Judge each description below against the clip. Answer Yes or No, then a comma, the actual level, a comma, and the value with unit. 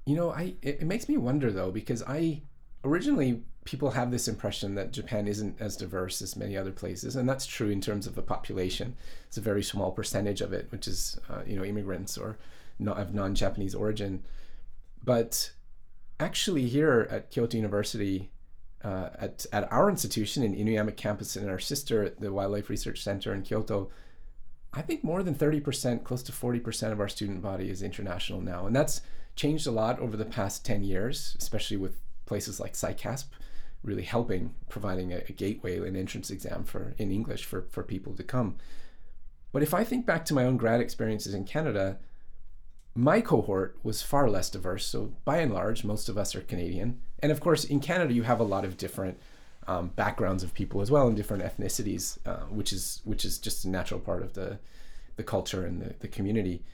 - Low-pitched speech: Yes, low, 105 Hz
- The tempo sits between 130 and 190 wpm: No, average, 200 wpm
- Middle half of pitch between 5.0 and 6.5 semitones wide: No, average, 4.3 semitones